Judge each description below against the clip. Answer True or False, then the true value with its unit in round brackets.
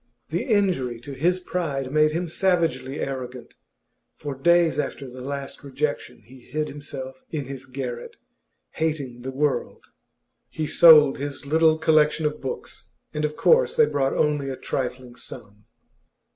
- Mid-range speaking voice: True (145 Hz)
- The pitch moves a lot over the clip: False (3.2 semitones)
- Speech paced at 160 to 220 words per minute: False (145 wpm)